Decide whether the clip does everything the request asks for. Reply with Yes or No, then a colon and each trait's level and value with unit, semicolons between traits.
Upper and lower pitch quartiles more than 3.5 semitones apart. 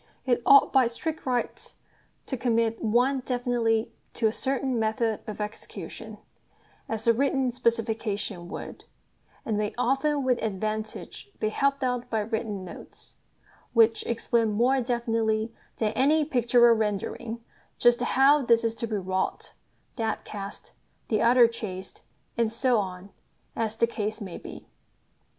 No: narrow, 2.4 semitones